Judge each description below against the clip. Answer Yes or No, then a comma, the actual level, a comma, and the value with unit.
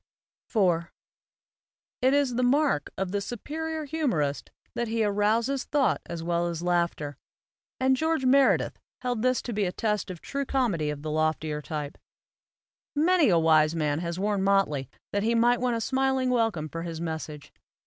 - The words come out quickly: No, average, 170 wpm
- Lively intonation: Yes, wide, 7.6 semitones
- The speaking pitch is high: Yes, high, 205 Hz